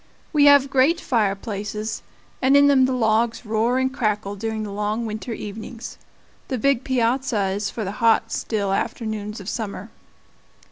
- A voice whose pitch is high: Yes, high, 225 Hz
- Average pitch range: Yes, average, 3.5 semitones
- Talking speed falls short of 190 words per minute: Yes, average, 155 wpm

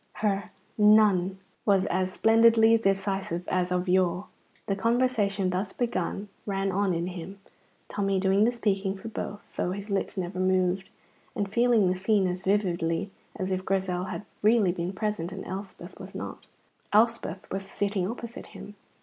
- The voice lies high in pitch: Yes, high, 195 Hz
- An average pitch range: No, narrow, 2.1 semitones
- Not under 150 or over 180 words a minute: Yes, average, 160 wpm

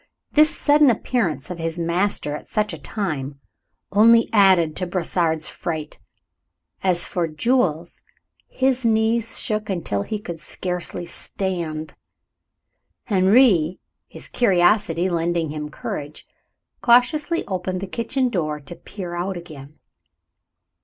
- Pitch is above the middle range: No, medium, 180 Hz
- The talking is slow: Yes, slow, 120 wpm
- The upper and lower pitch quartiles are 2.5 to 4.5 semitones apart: No, average, 5.0 semitones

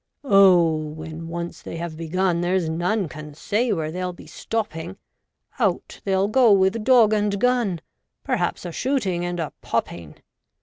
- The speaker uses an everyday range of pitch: Yes, average, 4.1 semitones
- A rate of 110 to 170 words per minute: Yes, average, 160 wpm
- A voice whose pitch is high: No, medium, 180 Hz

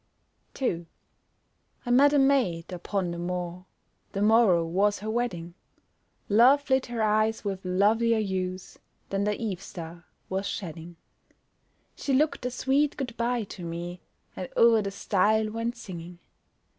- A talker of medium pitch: No, high, 205 Hz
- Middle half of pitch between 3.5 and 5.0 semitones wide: Yes, average, 4.7 semitones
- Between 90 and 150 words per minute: Yes, average, 145 wpm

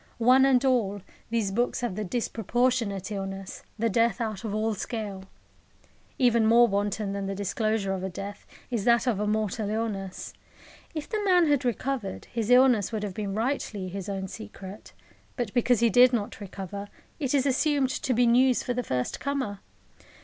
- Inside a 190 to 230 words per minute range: No, average, 180 wpm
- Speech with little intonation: No, average, 3.7 semitones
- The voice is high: Yes, high, 220 Hz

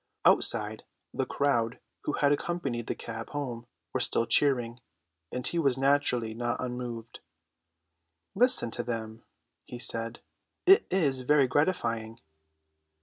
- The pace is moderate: No, slow, 125 wpm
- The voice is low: Yes, low, 125 Hz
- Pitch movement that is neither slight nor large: Yes, average, 3.7 semitones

